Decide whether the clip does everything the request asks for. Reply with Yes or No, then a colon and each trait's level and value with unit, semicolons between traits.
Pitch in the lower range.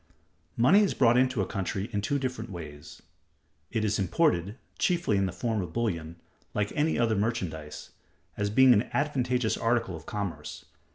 Yes: low, 110 Hz